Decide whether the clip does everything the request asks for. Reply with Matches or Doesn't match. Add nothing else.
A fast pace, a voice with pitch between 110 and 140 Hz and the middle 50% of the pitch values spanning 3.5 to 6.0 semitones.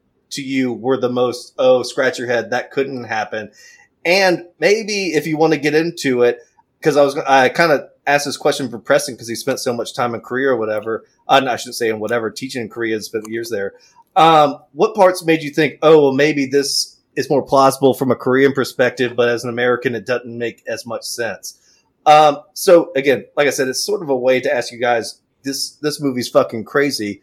Matches